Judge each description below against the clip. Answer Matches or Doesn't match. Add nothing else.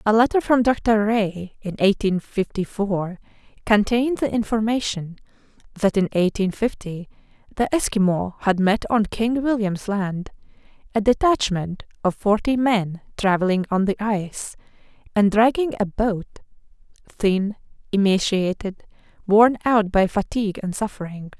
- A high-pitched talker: Matches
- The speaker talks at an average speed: Doesn't match